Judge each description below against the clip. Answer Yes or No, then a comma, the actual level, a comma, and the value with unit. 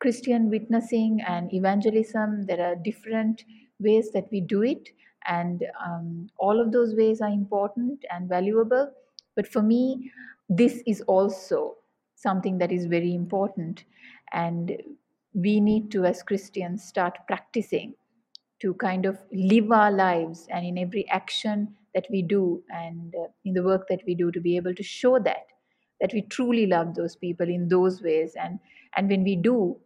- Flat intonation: No, average, 3.9 semitones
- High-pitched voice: Yes, high, 200 Hz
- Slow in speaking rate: No, average, 165 wpm